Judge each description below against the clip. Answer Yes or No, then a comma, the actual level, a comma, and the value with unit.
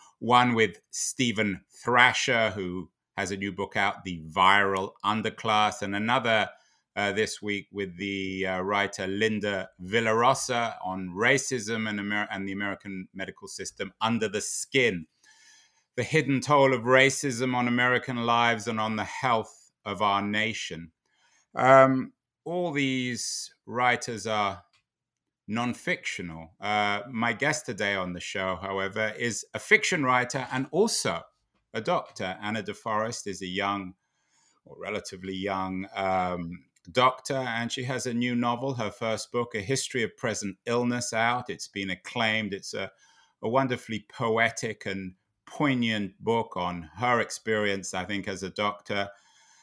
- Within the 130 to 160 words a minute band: Yes, average, 140 wpm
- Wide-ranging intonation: No, average, 4.0 semitones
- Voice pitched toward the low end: Yes, low, 110 Hz